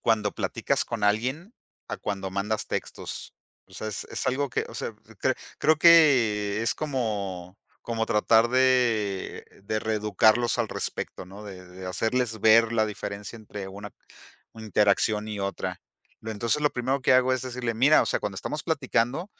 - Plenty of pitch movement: No, average, 3.5 semitones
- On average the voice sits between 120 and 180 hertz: No, low, 110 Hz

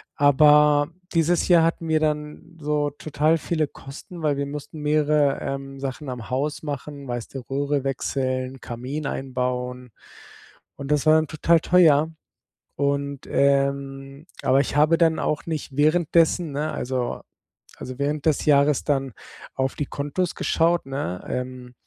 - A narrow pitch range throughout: Yes, narrow, 2.2 semitones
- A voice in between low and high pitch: Yes, medium, 145 Hz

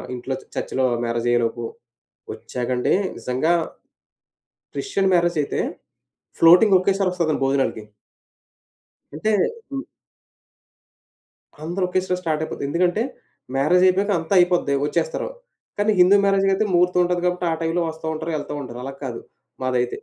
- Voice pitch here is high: No, medium, 175 Hz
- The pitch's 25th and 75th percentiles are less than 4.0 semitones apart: No, average, 5.3 semitones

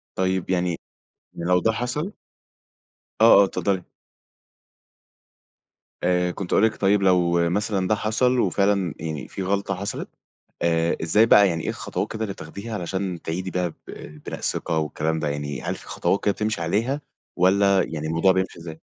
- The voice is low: Yes, very low, 95 Hz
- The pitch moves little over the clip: No, average, 3.2 semitones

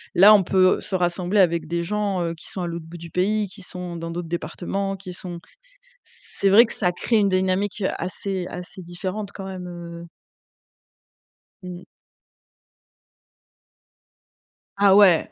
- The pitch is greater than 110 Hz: Yes, medium, 185 Hz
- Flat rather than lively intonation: Yes, narrow, 2.2 semitones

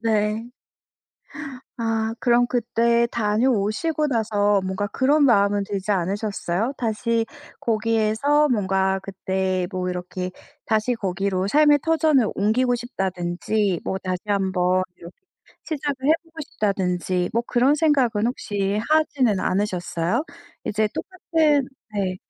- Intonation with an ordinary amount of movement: Yes, average, 4.3 semitones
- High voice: Yes, high, 215 Hz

